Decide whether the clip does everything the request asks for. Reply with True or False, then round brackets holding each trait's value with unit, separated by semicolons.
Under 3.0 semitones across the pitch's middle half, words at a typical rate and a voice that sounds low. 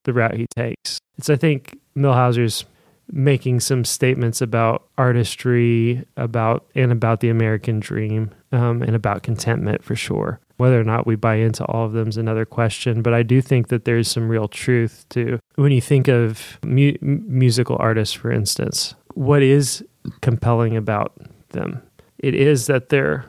True (2.6 semitones; 170 wpm; 120 Hz)